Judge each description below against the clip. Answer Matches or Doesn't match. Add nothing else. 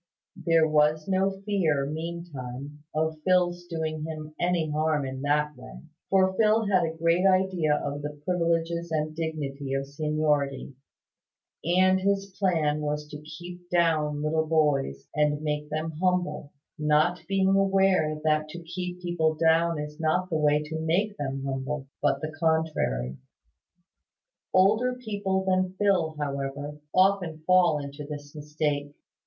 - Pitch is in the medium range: Matches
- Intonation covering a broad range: Doesn't match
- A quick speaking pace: Doesn't match